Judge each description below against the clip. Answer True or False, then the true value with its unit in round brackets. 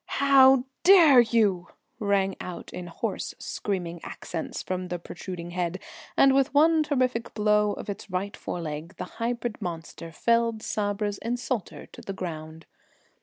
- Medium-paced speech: True (145 wpm)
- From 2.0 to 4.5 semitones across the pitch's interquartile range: False (5.4 semitones)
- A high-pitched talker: True (205 Hz)